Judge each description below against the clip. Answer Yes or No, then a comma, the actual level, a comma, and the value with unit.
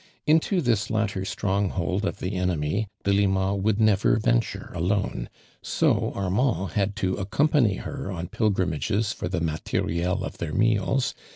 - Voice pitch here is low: Yes, low, 100 Hz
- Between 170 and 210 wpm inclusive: No, average, 145 wpm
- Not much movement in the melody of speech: No, average, 3.0 semitones